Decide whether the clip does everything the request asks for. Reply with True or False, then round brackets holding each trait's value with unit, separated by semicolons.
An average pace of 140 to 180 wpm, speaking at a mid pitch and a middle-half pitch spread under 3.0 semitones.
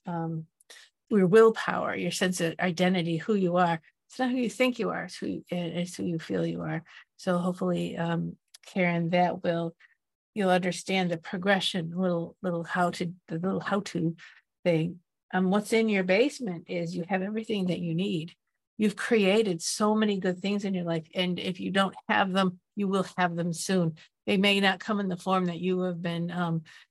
False (190 wpm; 180 Hz; 2.5 semitones)